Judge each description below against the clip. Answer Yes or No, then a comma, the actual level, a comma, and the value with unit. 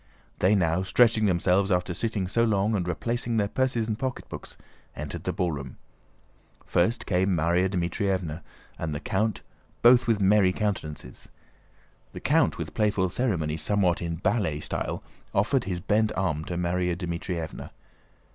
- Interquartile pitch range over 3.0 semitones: Yes, average, 3.7 semitones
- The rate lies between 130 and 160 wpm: Yes, average, 145 wpm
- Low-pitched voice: Yes, very low, 95 Hz